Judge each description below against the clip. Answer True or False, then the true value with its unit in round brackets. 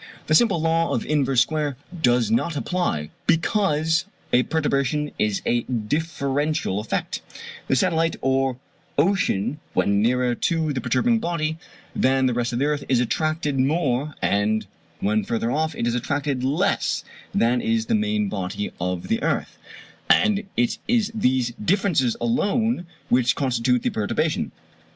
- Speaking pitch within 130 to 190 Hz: True (135 Hz)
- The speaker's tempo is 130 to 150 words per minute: True (145 wpm)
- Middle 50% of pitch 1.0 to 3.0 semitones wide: False (5.2 semitones)